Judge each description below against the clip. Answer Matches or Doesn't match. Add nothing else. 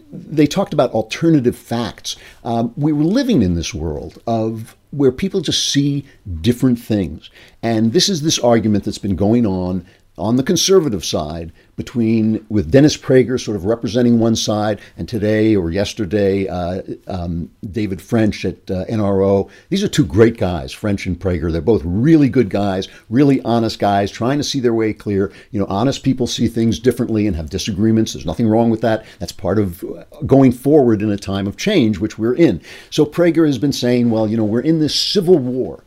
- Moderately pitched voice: Doesn't match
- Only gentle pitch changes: Doesn't match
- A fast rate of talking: Doesn't match